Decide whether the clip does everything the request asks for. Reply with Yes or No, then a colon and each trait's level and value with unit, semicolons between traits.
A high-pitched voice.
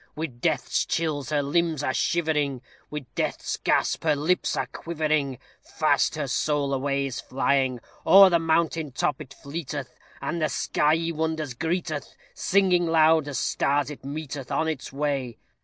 No: medium, 150 Hz